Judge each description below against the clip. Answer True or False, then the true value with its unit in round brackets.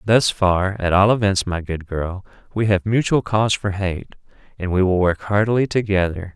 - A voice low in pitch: True (100 Hz)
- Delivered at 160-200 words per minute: True (190 wpm)